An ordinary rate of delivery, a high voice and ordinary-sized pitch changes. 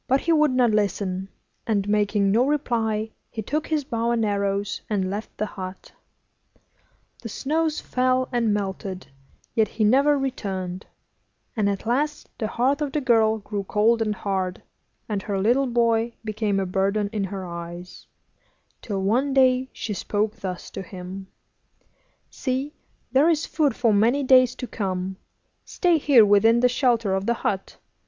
Yes: average, 160 wpm; high, 220 Hz; average, 4.3 semitones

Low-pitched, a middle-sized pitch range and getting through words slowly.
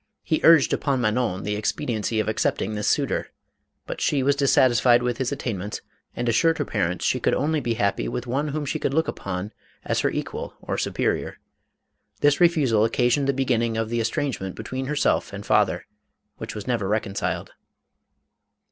No: low, 120 Hz; average, 4.5 semitones; average, 180 wpm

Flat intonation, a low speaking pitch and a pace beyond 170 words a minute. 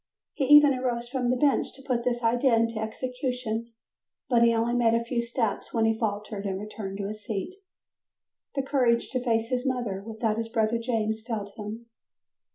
No: narrow, 2.3 semitones; high, 235 Hz; average, 185 wpm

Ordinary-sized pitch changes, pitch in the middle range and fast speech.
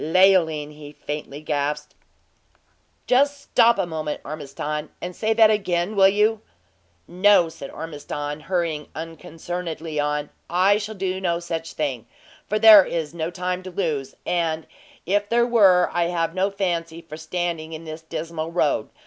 No: average, 3.5 semitones; medium, 170 Hz; average, 150 wpm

